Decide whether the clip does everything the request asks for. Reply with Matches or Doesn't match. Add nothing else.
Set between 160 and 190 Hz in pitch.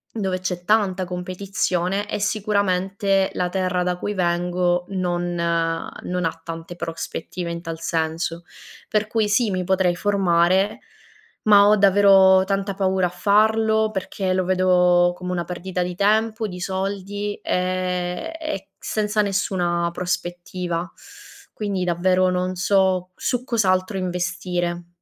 Matches